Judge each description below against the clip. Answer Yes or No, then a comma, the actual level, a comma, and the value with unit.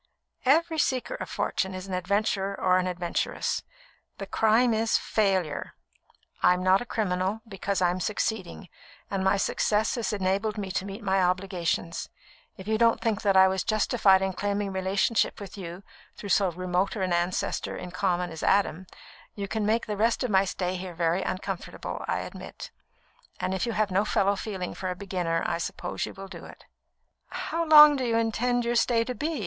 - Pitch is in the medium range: No, high, 195 Hz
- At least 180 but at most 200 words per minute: Yes, average, 185 wpm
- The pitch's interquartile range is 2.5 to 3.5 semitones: Yes, average, 3.0 semitones